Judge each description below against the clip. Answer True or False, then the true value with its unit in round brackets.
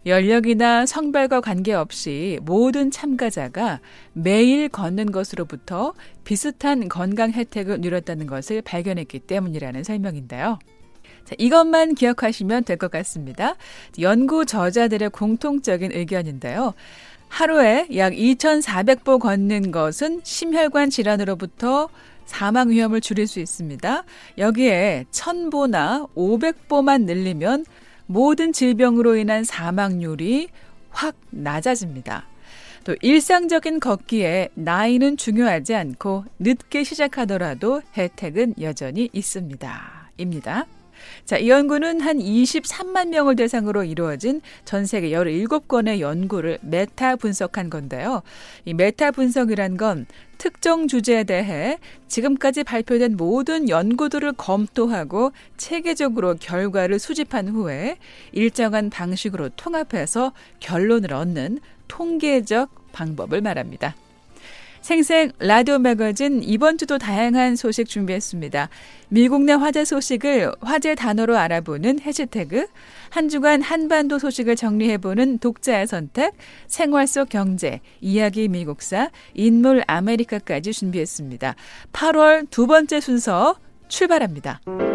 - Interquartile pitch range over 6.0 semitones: True (6.8 semitones)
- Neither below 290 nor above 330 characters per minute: False (270 characters per minute)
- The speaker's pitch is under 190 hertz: False (230 Hz)